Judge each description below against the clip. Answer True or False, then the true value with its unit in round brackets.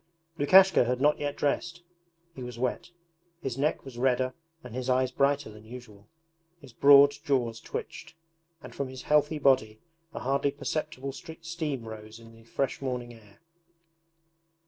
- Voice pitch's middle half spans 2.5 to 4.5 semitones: True (3.1 semitones)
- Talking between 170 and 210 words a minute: False (150 wpm)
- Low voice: True (130 Hz)